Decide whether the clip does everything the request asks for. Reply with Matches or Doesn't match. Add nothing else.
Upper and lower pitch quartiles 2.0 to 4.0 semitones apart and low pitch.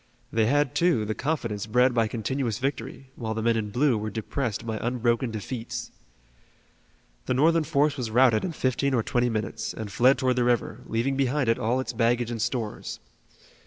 Matches